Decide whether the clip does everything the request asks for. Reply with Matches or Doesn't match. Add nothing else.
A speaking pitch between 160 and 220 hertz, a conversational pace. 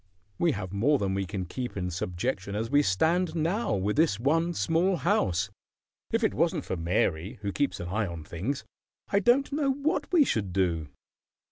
Doesn't match